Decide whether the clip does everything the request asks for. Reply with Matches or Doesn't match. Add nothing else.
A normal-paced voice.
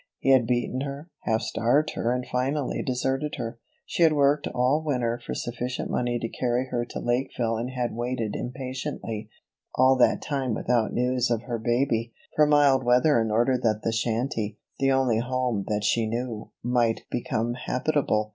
Matches